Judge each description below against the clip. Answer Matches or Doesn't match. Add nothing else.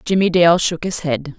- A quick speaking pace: Matches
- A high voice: Doesn't match